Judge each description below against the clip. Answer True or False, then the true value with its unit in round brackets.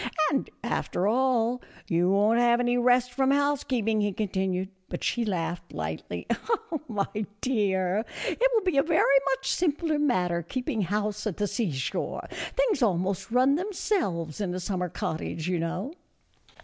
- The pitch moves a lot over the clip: True (6.5 semitones)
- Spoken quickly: False (155 wpm)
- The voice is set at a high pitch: True (220 Hz)